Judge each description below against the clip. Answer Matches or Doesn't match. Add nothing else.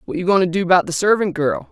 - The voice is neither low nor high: Matches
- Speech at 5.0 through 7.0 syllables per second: Matches